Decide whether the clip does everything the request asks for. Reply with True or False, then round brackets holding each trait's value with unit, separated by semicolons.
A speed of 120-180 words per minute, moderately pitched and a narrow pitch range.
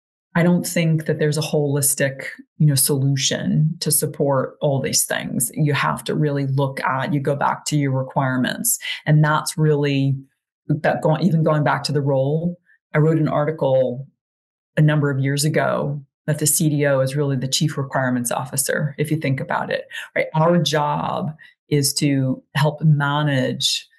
True (170 wpm; 150 Hz; 2.0 semitones)